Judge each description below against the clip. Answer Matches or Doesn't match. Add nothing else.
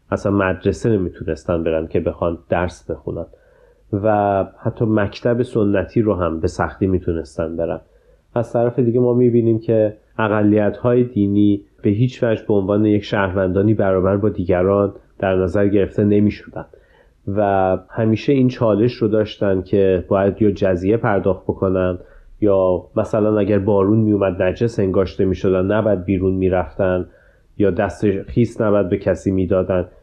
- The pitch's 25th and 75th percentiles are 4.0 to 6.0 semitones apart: Doesn't match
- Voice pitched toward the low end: Matches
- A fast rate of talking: Doesn't match